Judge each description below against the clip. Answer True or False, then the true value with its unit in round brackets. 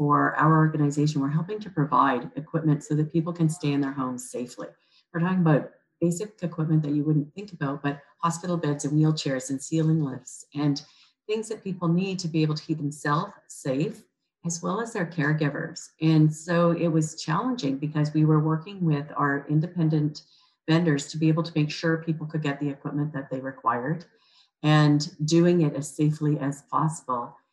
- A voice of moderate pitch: True (155 Hz)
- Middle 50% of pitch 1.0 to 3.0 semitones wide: True (2.5 semitones)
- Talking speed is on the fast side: False (185 wpm)